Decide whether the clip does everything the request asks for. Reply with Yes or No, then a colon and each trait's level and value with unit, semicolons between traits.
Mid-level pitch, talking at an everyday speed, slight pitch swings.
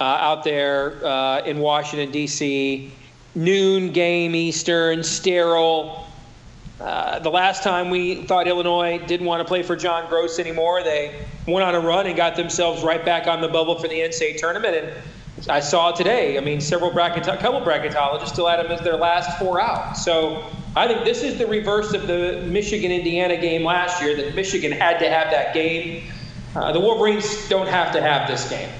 Yes: medium, 170 Hz; average, 190 wpm; narrow, 2.1 semitones